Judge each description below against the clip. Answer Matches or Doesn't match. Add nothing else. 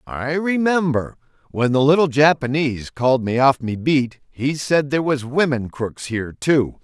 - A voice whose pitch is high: Doesn't match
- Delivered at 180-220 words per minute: Doesn't match